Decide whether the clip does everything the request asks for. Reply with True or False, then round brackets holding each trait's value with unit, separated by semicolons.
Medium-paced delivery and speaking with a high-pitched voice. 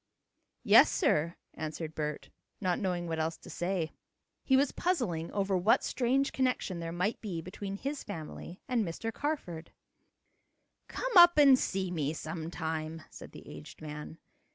False (150 wpm; 180 Hz)